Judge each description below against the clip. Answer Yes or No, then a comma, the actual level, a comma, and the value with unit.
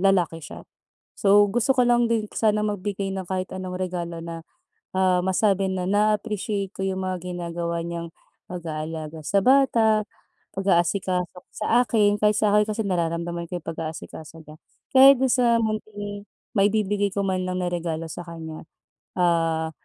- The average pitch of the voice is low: No, high, 190 Hz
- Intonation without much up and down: No, average, 3.7 semitones